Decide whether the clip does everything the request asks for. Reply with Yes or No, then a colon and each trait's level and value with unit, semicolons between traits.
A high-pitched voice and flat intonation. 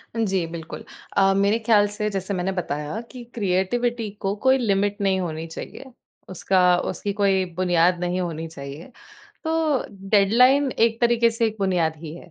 No: high, 195 Hz; average, 4.0 semitones